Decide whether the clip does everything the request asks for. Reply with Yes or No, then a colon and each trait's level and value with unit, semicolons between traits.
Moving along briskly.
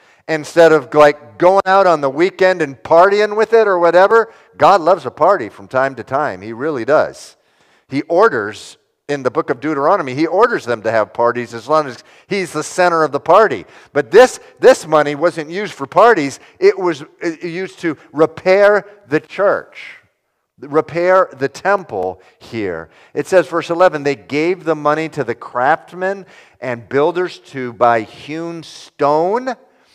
No: average, 170 wpm